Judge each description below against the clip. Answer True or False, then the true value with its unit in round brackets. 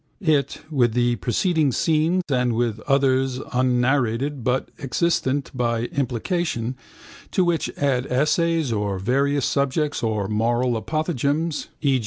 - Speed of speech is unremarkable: False (120 wpm)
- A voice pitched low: True (130 Hz)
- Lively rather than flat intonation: False (3.6 semitones)